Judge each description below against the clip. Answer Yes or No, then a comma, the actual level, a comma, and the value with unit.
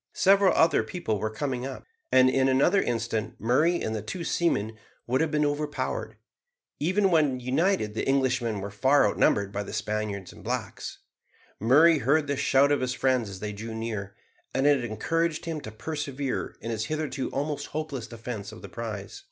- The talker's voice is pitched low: Yes, low, 130 Hz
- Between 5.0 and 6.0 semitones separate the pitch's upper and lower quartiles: Yes, wide, 5.4 semitones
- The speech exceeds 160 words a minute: Yes, average, 180 wpm